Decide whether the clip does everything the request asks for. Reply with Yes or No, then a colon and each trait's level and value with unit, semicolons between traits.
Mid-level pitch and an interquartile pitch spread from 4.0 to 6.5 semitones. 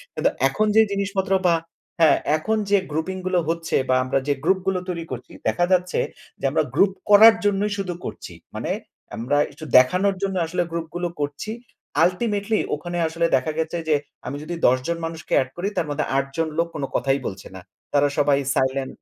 Yes: medium, 170 Hz; average, 4.8 semitones